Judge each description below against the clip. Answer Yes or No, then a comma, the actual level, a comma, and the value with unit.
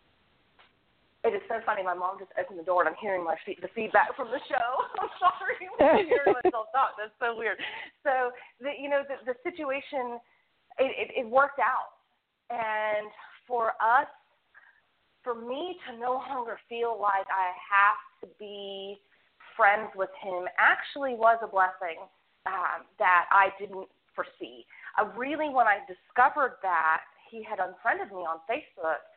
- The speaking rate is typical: Yes, average, 165 wpm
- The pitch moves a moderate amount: No, wide, 5.9 semitones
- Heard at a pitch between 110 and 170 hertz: No, high, 230 Hz